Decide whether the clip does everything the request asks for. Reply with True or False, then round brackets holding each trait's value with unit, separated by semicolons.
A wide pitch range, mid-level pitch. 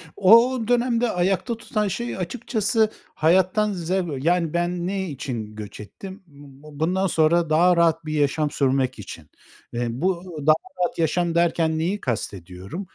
False (4.4 semitones; 170 Hz)